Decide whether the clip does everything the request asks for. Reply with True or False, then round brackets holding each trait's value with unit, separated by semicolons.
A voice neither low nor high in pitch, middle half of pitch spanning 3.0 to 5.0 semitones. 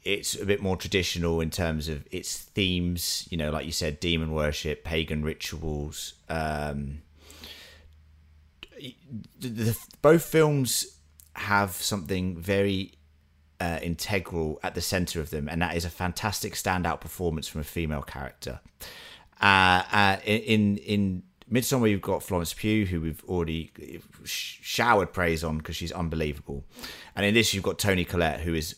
False (85 Hz; 4.1 semitones)